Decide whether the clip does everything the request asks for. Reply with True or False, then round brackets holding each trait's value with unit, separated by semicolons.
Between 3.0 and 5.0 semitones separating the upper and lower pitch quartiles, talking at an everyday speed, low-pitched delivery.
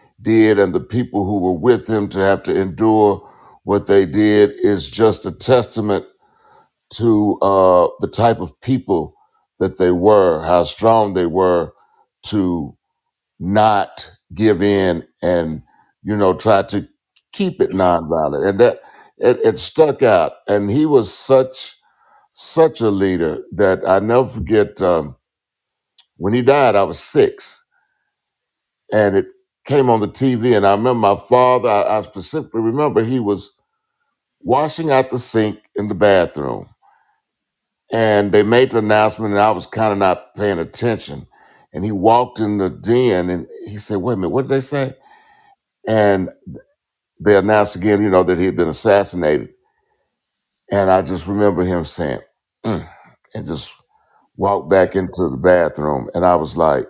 False (5.4 semitones; 160 wpm; 110 Hz)